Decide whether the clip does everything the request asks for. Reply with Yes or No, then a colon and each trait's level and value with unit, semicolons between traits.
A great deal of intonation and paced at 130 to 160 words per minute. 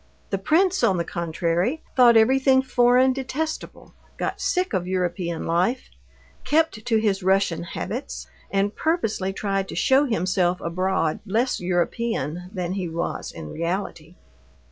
Yes: wide, 6.3 semitones; slow, 135 wpm